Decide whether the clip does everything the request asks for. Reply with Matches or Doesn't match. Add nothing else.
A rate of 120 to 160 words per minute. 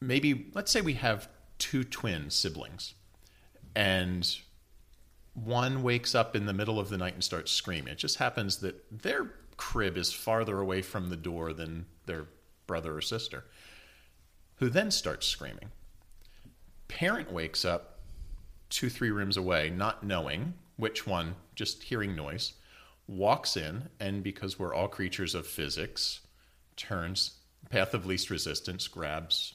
Matches